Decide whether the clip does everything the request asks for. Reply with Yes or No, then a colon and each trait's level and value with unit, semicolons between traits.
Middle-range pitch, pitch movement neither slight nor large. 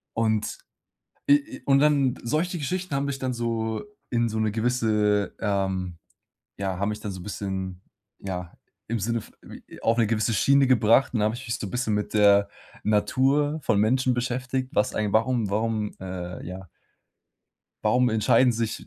No: low, 110 Hz; average, 3.8 semitones